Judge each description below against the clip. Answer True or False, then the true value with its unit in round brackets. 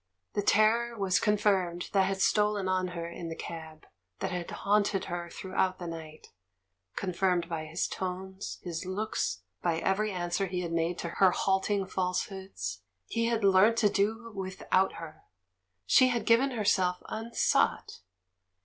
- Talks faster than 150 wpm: True (160 wpm)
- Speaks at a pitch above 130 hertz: True (190 Hz)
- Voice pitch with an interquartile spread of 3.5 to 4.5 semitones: False (3.1 semitones)